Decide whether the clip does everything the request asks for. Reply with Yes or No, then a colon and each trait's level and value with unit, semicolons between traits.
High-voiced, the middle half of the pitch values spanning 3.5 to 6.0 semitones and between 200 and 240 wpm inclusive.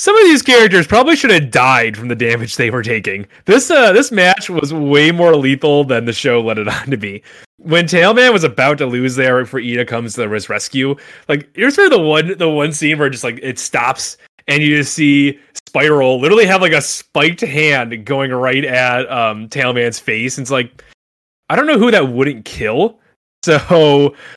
No: medium, 140 Hz; average, 4.7 semitones; fast, 205 wpm